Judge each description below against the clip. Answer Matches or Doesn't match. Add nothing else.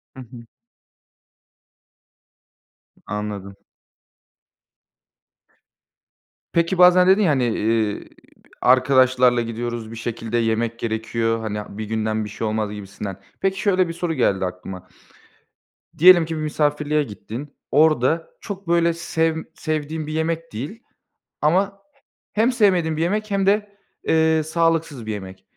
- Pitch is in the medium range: Matches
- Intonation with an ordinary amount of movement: Doesn't match